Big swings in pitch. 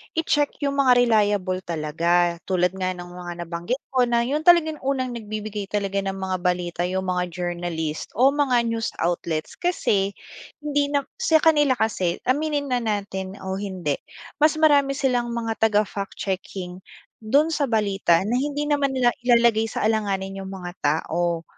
Yes: wide, 6.4 semitones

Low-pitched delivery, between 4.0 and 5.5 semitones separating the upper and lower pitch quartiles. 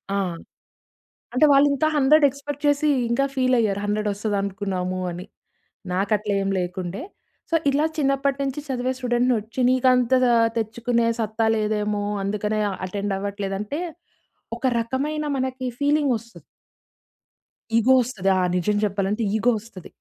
No: high, 230 Hz; average, 4.6 semitones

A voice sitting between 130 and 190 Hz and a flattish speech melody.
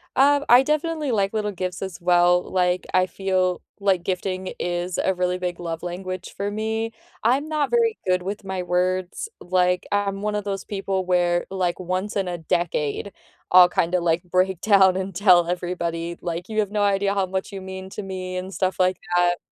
Yes: medium, 185 Hz; narrow, 2.1 semitones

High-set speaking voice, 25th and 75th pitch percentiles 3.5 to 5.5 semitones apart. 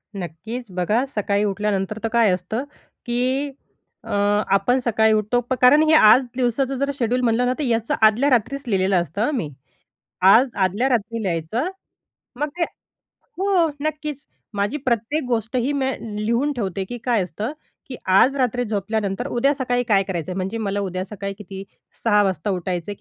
Yes: high, 225 Hz; average, 4.5 semitones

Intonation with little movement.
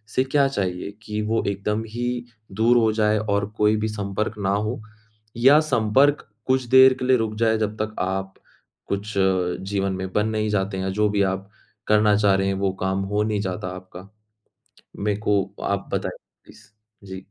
Yes: narrow, 2.3 semitones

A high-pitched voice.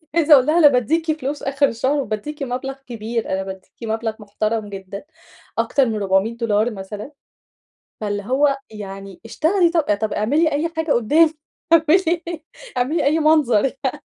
Yes: very high, 255 Hz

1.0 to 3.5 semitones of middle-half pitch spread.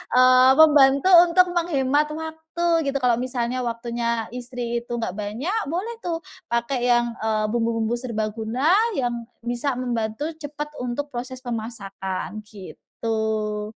No: average, 3.9 semitones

